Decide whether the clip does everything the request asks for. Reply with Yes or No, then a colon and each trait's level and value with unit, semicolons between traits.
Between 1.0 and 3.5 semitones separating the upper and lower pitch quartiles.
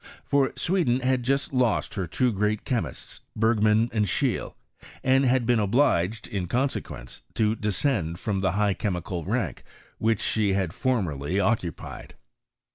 No: average, 4.5 semitones